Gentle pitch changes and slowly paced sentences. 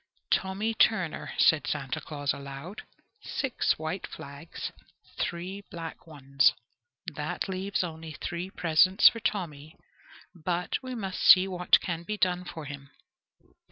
No: average, 3.9 semitones; slow, 125 wpm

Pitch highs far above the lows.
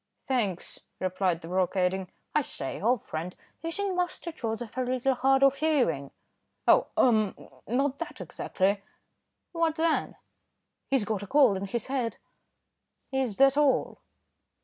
Yes: wide, 6.2 semitones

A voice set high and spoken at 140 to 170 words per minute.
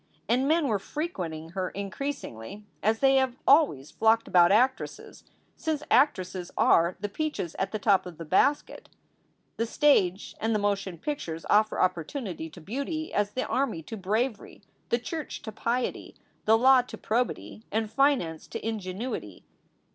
Yes: high, 220 Hz; average, 155 wpm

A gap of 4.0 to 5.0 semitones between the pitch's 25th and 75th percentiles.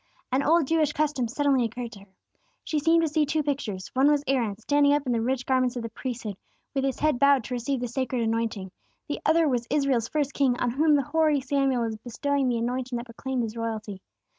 No: average, 3.6 semitones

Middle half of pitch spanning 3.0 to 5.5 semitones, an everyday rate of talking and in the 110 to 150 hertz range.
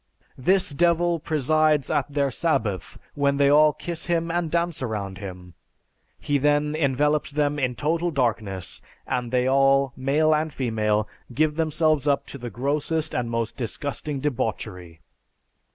Yes: average, 4.2 semitones; average, 145 wpm; medium, 140 Hz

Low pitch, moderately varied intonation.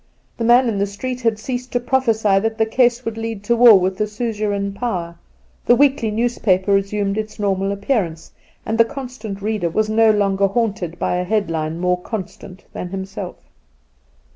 No: high, 210 Hz; average, 3.0 semitones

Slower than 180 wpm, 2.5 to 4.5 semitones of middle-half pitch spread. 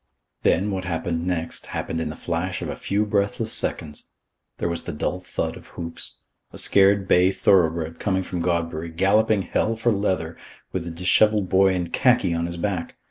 No: average, 185 wpm; average, 2.9 semitones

